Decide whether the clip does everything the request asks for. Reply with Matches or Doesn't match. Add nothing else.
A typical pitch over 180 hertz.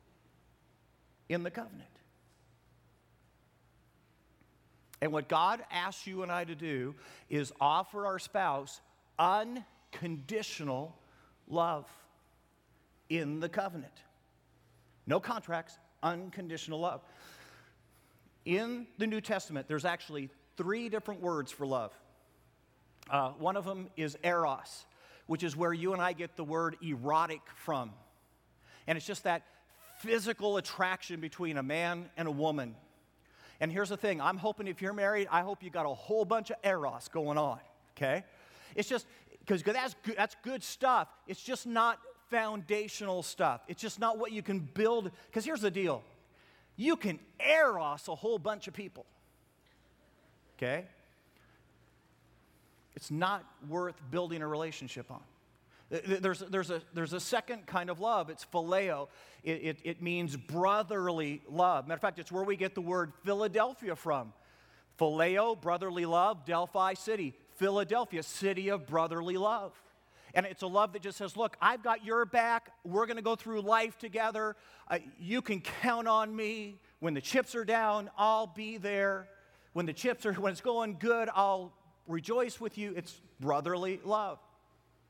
Matches